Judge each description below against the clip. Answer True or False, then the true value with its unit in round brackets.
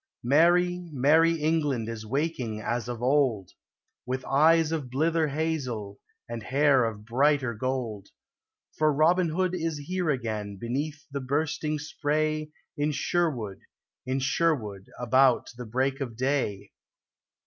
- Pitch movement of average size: True (4.6 semitones)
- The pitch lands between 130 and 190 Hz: True (140 Hz)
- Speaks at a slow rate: True (125 wpm)